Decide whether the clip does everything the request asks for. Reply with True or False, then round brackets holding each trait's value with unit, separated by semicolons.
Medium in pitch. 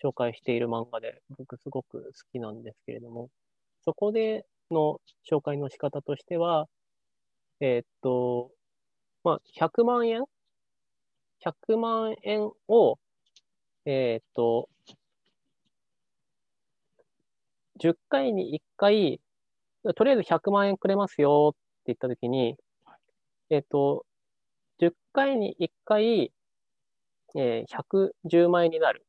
True (155 Hz)